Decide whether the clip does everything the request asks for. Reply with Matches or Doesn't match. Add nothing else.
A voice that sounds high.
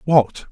Doesn't match